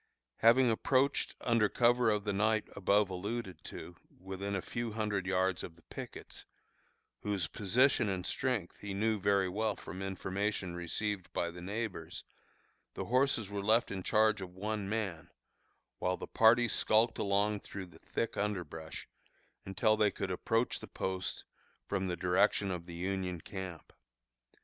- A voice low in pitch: Yes, low, 100 Hz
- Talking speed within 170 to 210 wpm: No, average, 155 wpm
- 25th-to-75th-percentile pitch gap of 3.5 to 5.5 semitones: No, average, 2.8 semitones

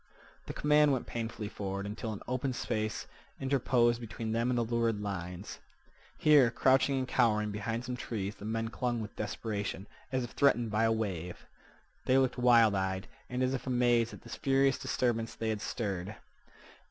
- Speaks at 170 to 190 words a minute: Yes, average, 175 wpm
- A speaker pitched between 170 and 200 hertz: No, low, 115 Hz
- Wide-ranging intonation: No, average, 3.0 semitones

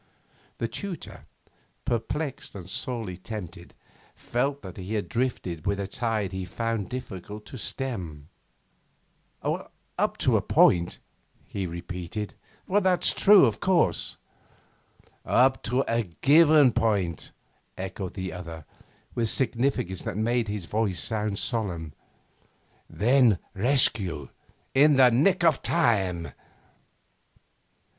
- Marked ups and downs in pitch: Yes, wide, 5.7 semitones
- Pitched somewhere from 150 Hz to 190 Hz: No, low, 110 Hz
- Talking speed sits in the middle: No, slow, 110 wpm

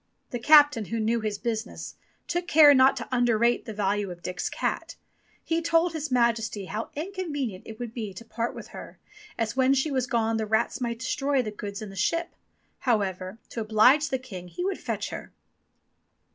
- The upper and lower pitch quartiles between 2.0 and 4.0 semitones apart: No, average, 4.4 semitones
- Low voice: No, high, 235 Hz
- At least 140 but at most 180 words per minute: No, average, 190 wpm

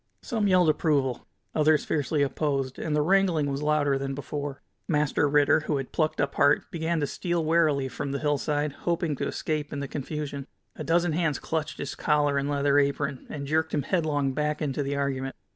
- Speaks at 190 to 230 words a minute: Yes, average, 195 wpm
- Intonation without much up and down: Yes, narrow, 2.0 semitones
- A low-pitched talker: No, medium, 145 Hz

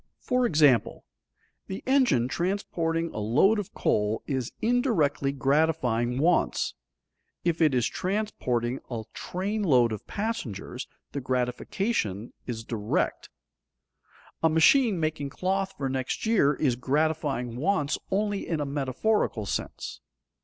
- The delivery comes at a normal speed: No, slow, 120 wpm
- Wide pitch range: Yes, wide, 7.5 semitones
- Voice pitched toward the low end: No, medium, 150 Hz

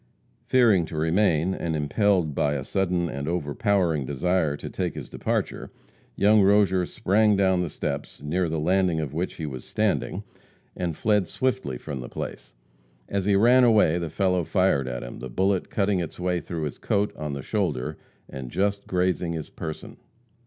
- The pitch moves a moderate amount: Yes, average, 4.5 semitones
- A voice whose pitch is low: Yes, very low, 90 Hz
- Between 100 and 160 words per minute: No, average, 175 wpm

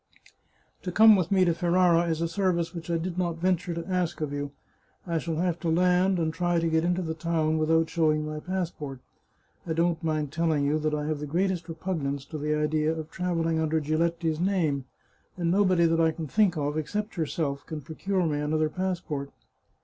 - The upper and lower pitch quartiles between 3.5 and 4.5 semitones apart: No, narrow, 2.4 semitones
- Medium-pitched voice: Yes, medium, 165 Hz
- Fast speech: Yes, fast, 210 wpm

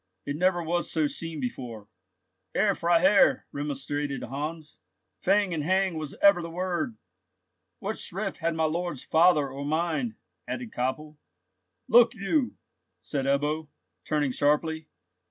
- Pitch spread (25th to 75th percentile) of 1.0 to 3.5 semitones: No, average, 4.0 semitones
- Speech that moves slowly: Yes, slow, 130 wpm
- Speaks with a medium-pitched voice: Yes, medium, 160 Hz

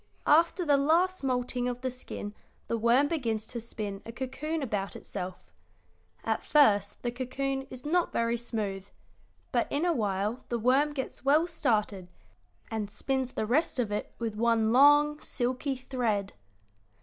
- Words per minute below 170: Yes, average, 155 wpm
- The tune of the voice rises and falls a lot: No, average, 4.4 semitones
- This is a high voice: Yes, very high, 250 Hz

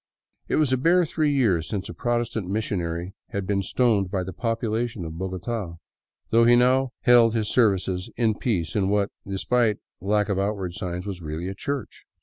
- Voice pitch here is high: No, low, 105 Hz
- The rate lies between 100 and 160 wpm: No, average, 185 wpm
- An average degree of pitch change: Yes, average, 4.2 semitones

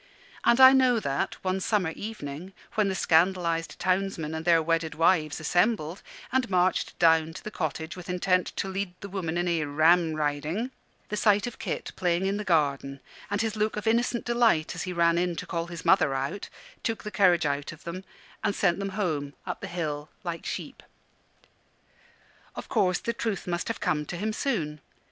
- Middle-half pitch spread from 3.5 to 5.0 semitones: Yes, average, 4.0 semitones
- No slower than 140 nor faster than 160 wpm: No, average, 190 wpm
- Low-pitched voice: No, medium, 180 Hz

